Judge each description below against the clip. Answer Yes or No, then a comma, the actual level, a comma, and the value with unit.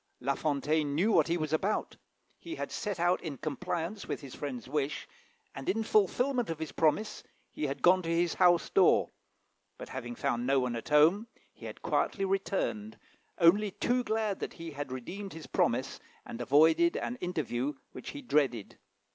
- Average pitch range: No, wide, 6.0 semitones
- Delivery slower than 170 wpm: No, average, 180 wpm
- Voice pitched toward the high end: No, medium, 165 Hz